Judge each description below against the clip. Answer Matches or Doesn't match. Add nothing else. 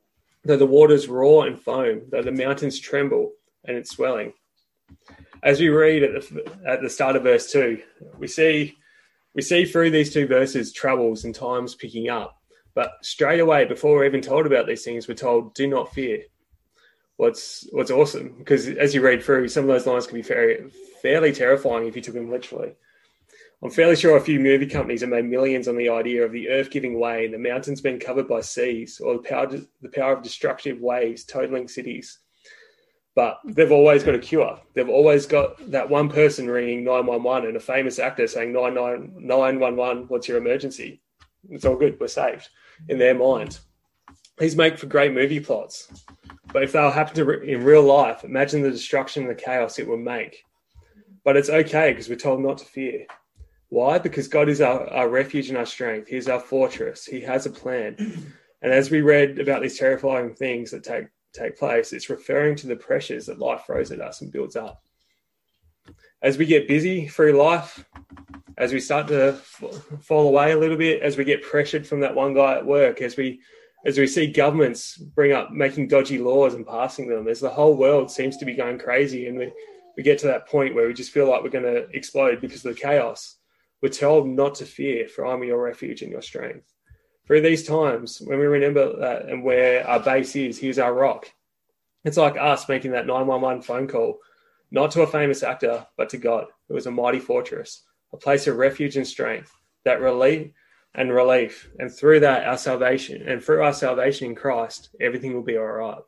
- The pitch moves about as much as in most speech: Matches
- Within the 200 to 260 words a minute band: Matches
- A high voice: Doesn't match